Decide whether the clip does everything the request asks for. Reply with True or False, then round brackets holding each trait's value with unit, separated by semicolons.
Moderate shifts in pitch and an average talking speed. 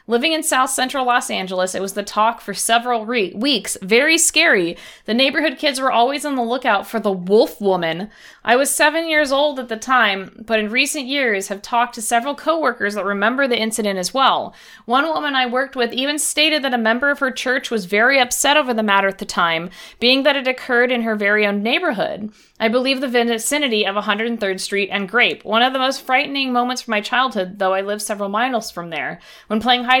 False (4.2 semitones; 220 wpm)